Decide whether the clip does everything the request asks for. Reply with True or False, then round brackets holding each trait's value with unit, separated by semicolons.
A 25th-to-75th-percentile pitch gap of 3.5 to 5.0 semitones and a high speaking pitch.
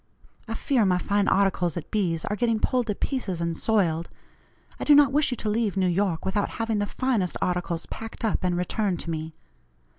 True (4.2 semitones; 200 Hz)